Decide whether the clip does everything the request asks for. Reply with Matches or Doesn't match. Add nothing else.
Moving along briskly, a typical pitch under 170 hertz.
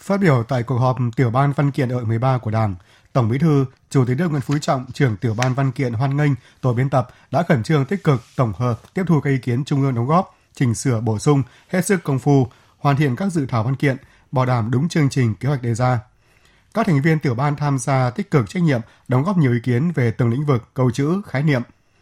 Matches